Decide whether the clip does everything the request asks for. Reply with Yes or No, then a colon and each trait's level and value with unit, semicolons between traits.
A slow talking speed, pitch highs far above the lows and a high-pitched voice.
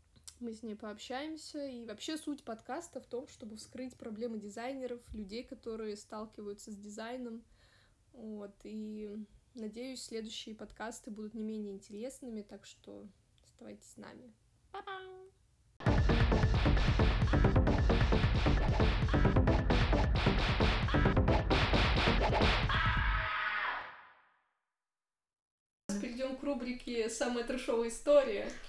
No: slow, 80 wpm; average, 3.2 semitones; high, 230 Hz